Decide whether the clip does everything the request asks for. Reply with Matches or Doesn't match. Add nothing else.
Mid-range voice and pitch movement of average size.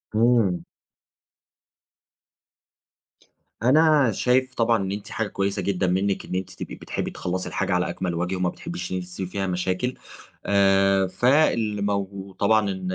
Doesn't match